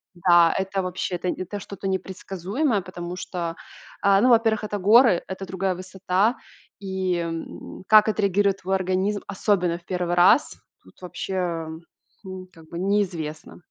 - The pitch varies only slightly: Yes, narrow, 2.1 semitones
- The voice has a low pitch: No, medium, 185 Hz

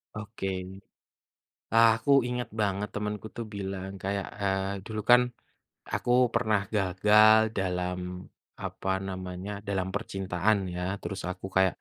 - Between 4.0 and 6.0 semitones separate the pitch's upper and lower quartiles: No, narrow, 2.4 semitones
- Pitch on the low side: Yes, low, 100 Hz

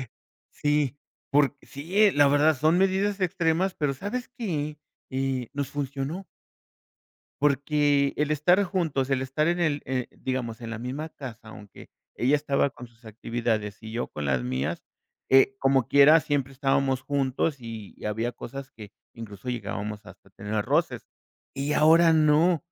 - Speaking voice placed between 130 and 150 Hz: Yes, medium, 140 Hz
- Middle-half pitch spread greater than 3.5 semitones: Yes, average, 4.1 semitones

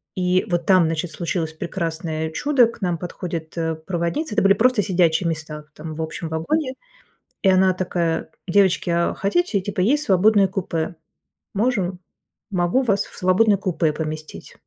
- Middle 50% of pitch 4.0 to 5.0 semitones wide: No, average, 3.5 semitones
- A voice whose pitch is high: No, medium, 180 Hz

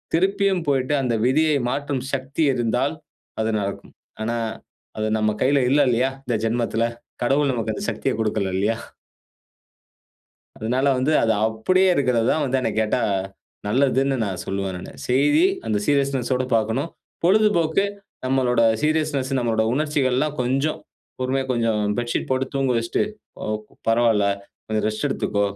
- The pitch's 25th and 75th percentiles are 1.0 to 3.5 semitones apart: No, average, 4.1 semitones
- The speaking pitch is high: No, low, 130 Hz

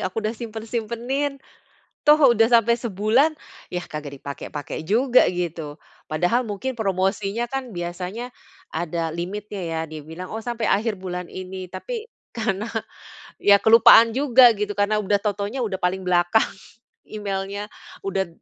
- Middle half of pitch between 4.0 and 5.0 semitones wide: Yes, average, 4.3 semitones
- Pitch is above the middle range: Yes, high, 205 Hz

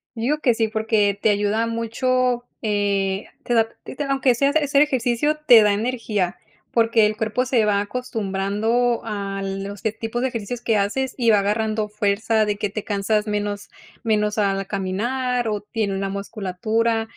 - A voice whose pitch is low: No, high, 220 Hz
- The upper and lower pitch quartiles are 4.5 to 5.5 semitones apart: No, average, 2.9 semitones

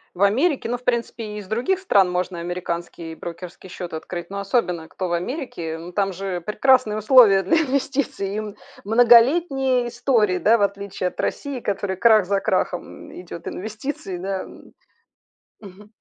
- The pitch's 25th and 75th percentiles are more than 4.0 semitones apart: Yes, average, 5.1 semitones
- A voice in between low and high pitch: No, high, 200 Hz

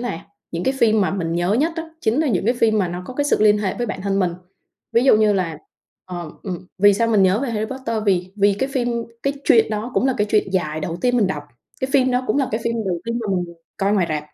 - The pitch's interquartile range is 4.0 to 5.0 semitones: Yes, average, 4.7 semitones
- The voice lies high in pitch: Yes, high, 210 Hz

